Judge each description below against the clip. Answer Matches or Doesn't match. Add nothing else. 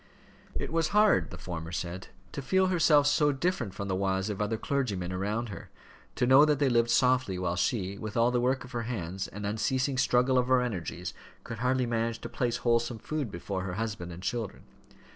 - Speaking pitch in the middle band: Doesn't match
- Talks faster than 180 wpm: Matches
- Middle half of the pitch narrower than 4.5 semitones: Doesn't match